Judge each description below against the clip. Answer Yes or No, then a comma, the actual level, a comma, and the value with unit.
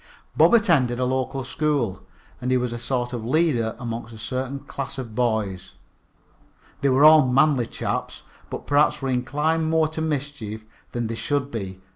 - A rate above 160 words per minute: Yes, average, 170 wpm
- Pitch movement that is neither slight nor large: Yes, average, 3.7 semitones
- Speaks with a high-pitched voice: No, low, 130 Hz